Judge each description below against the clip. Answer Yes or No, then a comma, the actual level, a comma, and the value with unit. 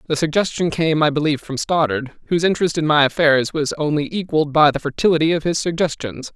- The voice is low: No, medium, 155 Hz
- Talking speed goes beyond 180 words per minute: Yes, average, 200 wpm